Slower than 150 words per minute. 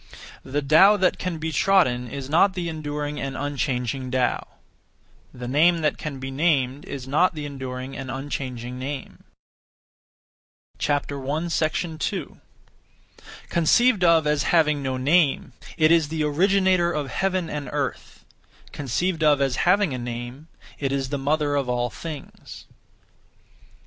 Yes: slow, 135 wpm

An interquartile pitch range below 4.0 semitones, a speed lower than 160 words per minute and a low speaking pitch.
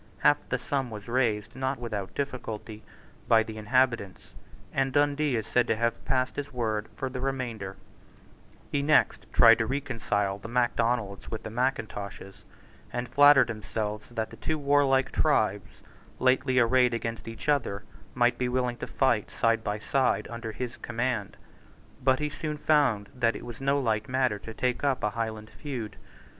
No: average, 3.3 semitones; average, 165 wpm; low, 120 Hz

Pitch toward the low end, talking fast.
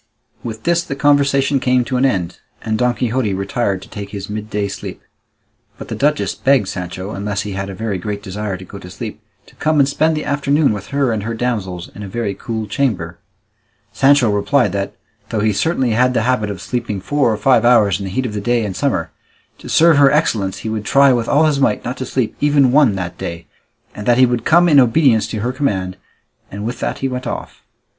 Yes: low, 115 Hz; fast, 225 wpm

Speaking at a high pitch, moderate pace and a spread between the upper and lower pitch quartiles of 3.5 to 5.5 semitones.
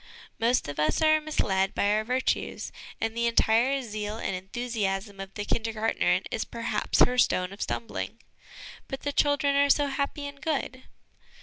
Yes: high, 235 Hz; average, 170 wpm; average, 5.2 semitones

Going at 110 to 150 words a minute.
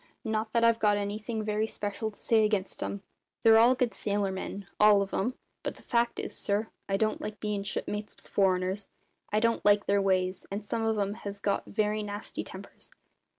No: average, 195 wpm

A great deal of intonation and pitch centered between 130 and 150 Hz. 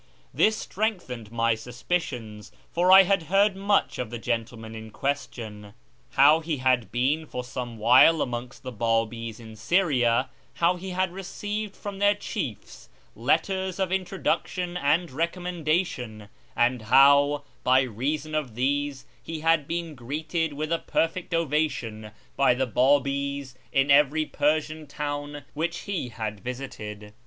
Yes: wide, 5.7 semitones; medium, 140 Hz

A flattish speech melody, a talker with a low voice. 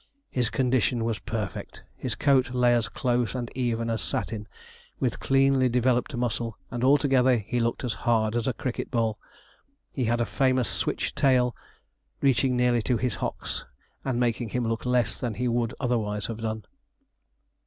Yes: narrow, 1.9 semitones; low, 120 Hz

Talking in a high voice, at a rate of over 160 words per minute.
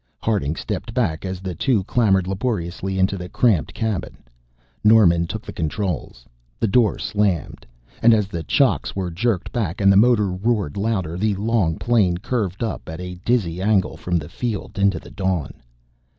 No: very low, 95 Hz; average, 170 wpm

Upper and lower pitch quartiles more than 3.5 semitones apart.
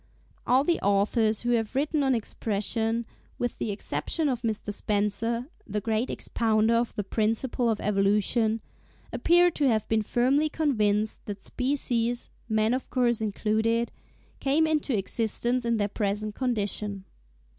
No: average, 3.0 semitones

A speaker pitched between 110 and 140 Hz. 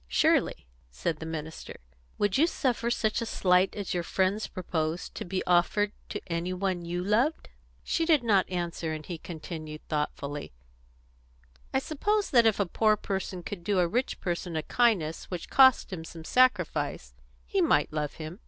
No: medium, 180 Hz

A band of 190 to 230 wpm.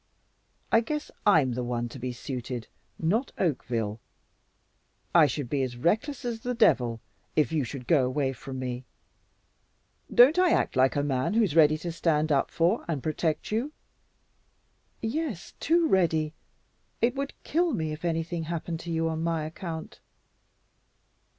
No: average, 155 wpm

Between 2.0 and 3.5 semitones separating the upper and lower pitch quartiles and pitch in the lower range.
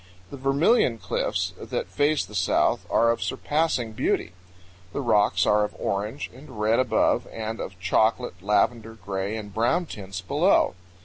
No: average, 4.4 semitones; low, 110 Hz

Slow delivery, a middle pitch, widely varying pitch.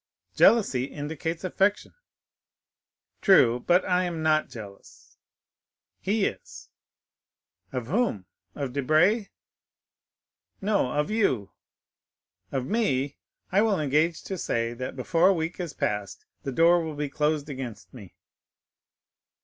Yes: slow, 115 wpm; medium, 155 Hz; wide, 6.2 semitones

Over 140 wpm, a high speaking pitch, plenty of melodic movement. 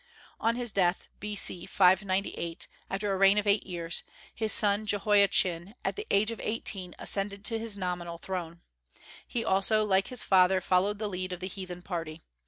No: average, 170 wpm; high, 195 Hz; narrow, 2.5 semitones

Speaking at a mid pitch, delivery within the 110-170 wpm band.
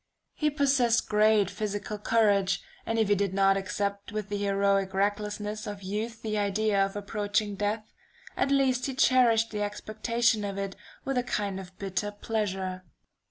No: high, 205 Hz; average, 160 wpm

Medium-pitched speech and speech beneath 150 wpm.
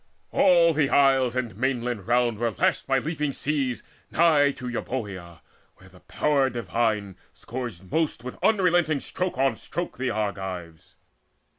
No: low, 125 Hz; average, 140 wpm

